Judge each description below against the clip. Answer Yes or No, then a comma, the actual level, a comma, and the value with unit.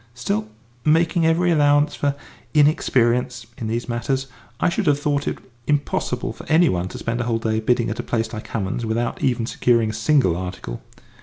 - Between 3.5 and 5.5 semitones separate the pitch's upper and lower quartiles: Yes, average, 4.5 semitones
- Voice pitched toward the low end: Yes, low, 120 Hz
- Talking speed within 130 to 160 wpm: No, average, 185 wpm